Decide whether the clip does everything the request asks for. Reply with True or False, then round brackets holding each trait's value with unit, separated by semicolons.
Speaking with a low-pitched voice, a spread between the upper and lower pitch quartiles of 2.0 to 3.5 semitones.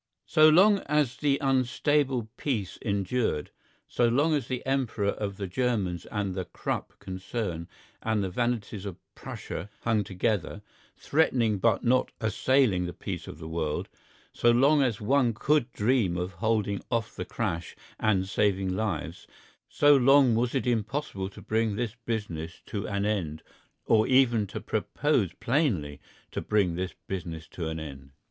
False (110 Hz; 5.3 semitones)